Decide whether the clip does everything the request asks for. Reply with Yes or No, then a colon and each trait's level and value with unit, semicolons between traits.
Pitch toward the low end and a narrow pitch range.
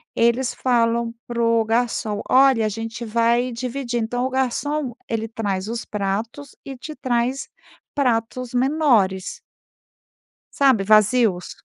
No: high, 235 Hz; narrow, 2.3 semitones